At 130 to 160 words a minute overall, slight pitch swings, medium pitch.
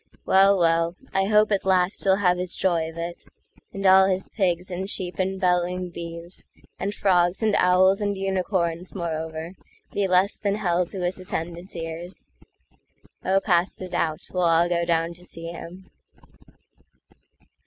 Yes: average, 145 wpm; narrow, 2.0 semitones; medium, 180 Hz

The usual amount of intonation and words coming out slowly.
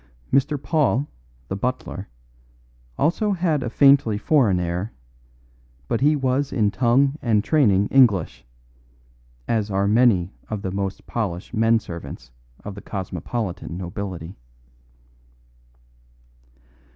No: wide, 5.7 semitones; slow, 110 wpm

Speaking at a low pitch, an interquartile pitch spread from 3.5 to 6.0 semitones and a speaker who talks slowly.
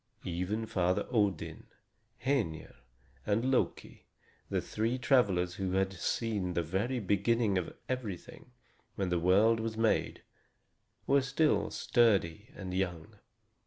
Yes: low, 100 Hz; average, 4.1 semitones; slow, 120 wpm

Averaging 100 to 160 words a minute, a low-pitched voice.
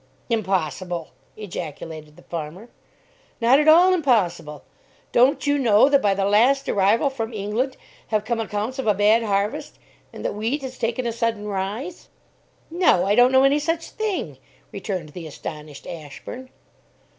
No: average, 155 wpm; high, 220 Hz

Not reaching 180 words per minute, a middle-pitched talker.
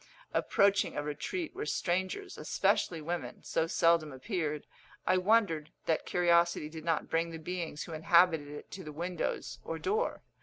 Yes: average, 155 wpm; medium, 170 Hz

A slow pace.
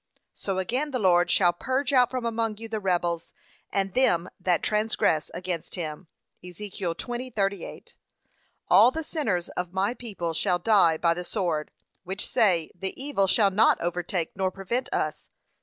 No: average, 155 wpm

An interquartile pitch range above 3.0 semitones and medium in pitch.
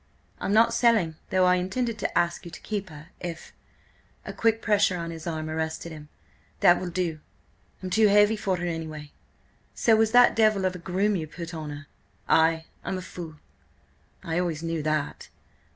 Yes: average, 4.2 semitones; medium, 175 Hz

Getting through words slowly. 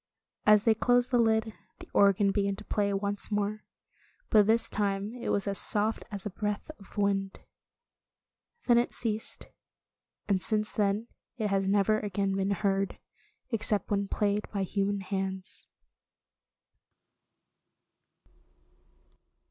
Yes: slow, 130 wpm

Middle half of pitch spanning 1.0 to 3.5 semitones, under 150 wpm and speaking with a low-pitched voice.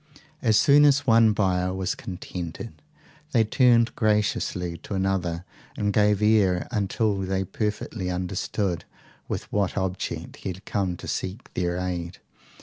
Yes: average, 2.9 semitones; average, 140 wpm; very low, 95 Hz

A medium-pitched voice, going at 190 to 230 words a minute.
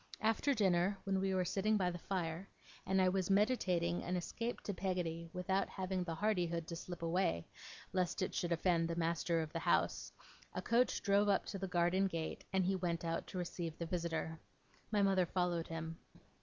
Yes: medium, 180 Hz; average, 195 wpm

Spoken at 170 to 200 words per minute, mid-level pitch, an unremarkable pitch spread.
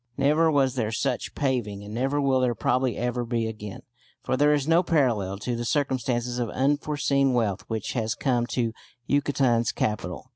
No: average, 175 wpm; low, 125 Hz; average, 3.3 semitones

